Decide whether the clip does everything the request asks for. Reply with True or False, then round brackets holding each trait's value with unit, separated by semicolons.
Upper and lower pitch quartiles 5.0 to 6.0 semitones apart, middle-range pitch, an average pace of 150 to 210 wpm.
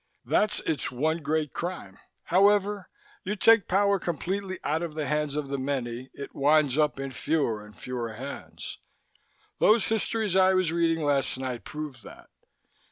True (5.4 semitones; 155 Hz; 160 wpm)